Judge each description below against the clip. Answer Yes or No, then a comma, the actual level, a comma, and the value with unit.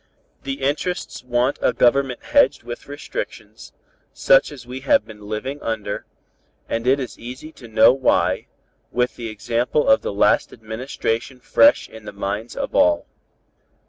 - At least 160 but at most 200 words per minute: No, average, 150 wpm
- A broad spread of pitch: No, average, 3.6 semitones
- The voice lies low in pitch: Yes, low, 125 Hz